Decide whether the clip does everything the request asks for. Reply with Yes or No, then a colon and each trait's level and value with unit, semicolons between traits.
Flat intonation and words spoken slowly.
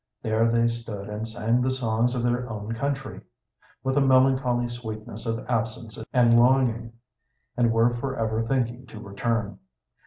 No: narrow, 1.8 semitones; average, 150 wpm